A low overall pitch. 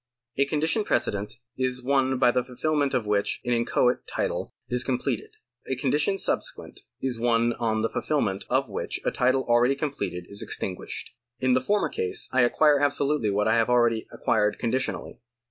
Yes: low, 125 Hz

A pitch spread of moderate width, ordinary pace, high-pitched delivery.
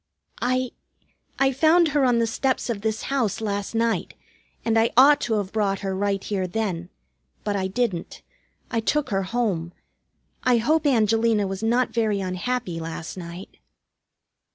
Yes: average, 4.2 semitones; average, 155 wpm; high, 220 Hz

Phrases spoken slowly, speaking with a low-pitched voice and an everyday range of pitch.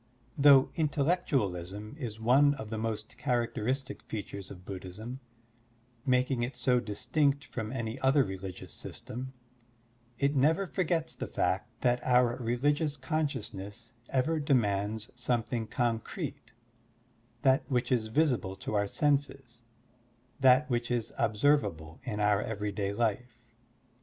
Yes: slow, 125 wpm; low, 120 Hz; average, 4.4 semitones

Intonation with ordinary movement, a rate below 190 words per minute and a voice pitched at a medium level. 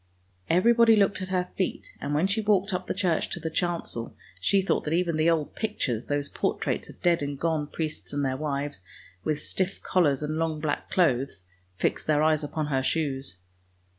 No: average, 4.1 semitones; average, 195 wpm; medium, 160 Hz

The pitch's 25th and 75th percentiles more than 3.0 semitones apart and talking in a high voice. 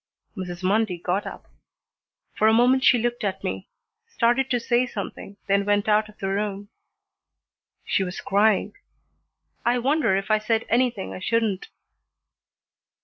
Yes: average, 3.5 semitones; high, 215 Hz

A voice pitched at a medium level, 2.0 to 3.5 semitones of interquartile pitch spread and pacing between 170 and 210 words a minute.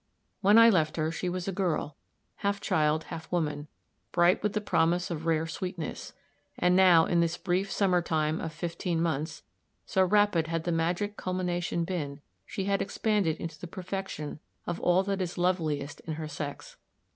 Yes: medium, 175 Hz; average, 2.8 semitones; average, 175 wpm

